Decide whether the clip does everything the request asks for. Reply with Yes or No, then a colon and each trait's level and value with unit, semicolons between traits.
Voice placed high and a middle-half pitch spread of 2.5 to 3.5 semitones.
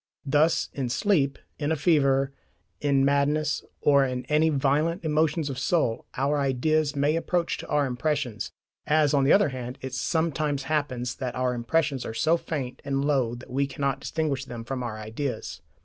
No: medium, 140 Hz; average, 2.9 semitones